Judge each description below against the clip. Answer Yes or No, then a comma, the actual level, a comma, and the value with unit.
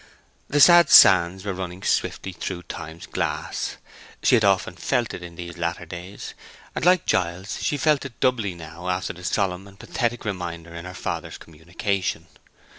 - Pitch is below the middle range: Yes, very low, 90 Hz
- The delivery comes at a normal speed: Yes, average, 170 wpm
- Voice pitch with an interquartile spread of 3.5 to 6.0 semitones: No, average, 3.0 semitones